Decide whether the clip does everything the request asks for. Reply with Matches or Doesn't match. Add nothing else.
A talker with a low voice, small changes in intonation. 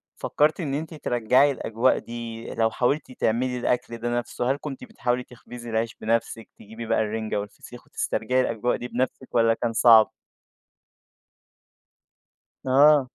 Matches